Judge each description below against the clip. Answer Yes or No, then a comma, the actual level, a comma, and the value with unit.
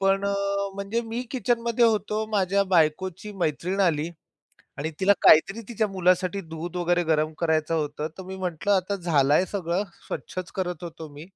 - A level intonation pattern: No, average, 3.6 semitones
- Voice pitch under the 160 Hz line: No, medium, 185 Hz